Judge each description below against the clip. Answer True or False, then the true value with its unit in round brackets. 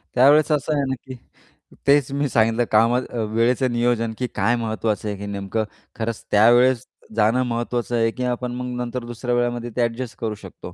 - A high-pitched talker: False (120 Hz)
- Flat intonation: True (2.0 semitones)